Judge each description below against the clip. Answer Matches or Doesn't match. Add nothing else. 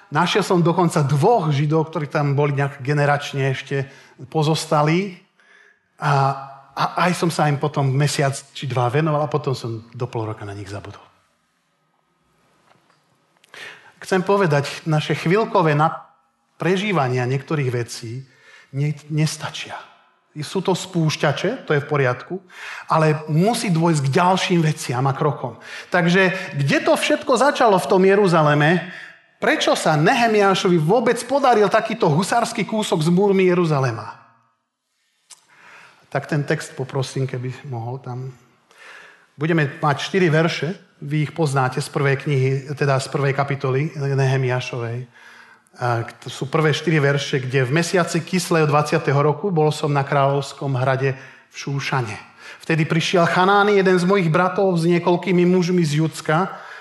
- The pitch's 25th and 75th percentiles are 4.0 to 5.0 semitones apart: Matches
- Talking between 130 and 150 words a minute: Matches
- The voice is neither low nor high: Matches